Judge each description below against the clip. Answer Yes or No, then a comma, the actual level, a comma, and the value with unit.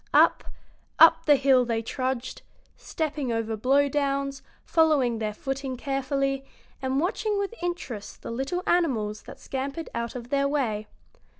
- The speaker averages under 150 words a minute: Yes, average, 140 wpm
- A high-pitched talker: Yes, very high, 270 Hz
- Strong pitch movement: No, average, 3.5 semitones